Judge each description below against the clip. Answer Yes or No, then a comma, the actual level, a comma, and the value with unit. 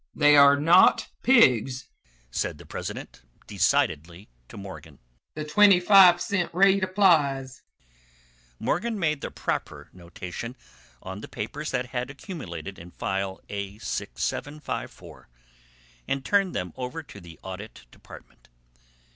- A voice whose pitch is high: No, low, 135 Hz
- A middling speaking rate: No, slow, 120 wpm